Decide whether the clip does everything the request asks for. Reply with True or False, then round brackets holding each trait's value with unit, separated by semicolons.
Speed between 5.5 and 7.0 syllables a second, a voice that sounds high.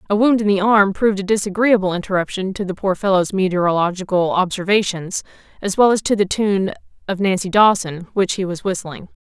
True (5.8 syllables/s; 195 Hz)